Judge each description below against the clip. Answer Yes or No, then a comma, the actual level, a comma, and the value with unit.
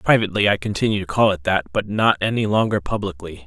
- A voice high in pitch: No, low, 100 Hz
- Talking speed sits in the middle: No, fast, 210 wpm